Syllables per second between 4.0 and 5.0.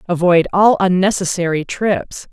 Yes: 4.4 syllables/s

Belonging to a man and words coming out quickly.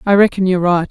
No: female; fast, 265 wpm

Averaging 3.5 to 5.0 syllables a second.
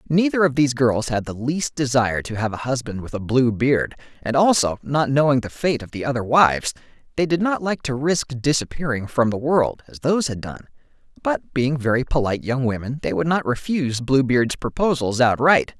No: 5.4 syllables/s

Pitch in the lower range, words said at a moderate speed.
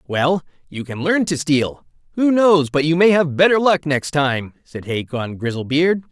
No: medium, 155 Hz; average, 185 wpm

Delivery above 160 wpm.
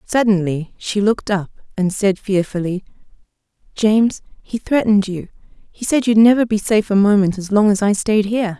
Yes: average, 175 wpm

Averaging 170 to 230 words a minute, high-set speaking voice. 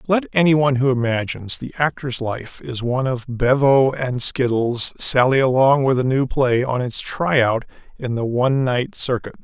No: average, 185 wpm; low, 130 Hz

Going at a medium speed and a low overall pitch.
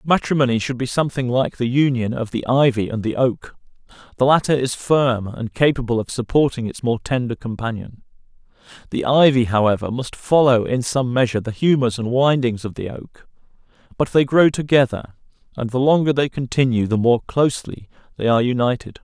Yes: average, 175 wpm; low, 125 Hz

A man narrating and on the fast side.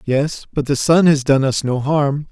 Yes: male; fast, 235 wpm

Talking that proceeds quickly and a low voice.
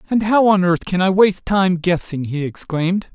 No: fast, 210 wpm; medium, 185 Hz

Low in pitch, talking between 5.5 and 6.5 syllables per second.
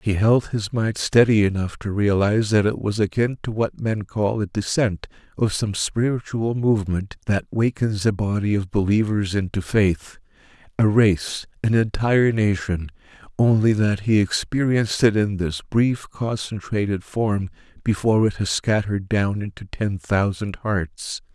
No: low, 105 Hz; 4.5 syllables/s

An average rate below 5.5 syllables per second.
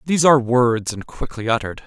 No: 6.4 syllables/s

